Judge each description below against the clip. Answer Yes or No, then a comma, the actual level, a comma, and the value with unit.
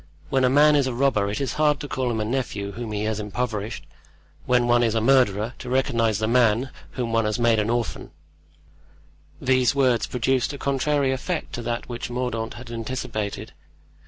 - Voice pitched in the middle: No, low, 120 Hz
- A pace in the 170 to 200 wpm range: Yes, average, 190 wpm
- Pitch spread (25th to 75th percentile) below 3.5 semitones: Yes, average, 2.9 semitones